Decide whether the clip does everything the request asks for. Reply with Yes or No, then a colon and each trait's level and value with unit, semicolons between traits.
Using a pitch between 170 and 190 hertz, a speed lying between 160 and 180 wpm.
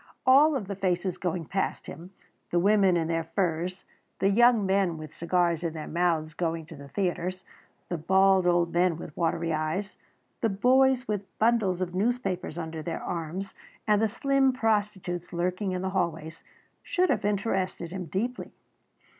Yes: medium, 185 Hz; average, 165 wpm